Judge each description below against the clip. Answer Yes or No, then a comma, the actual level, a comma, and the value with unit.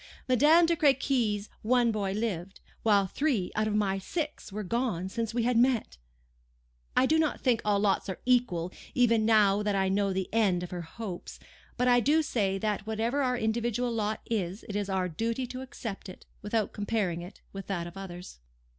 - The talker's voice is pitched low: No, high, 215 Hz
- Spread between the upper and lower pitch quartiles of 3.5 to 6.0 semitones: Yes, average, 4.0 semitones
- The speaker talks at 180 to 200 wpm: Yes, average, 190 wpm